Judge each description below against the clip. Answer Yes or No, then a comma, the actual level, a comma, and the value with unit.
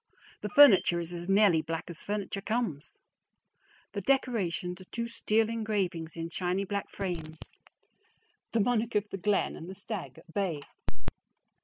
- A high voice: Yes, high, 195 Hz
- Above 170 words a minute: No, average, 150 wpm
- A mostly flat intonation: No, average, 4.0 semitones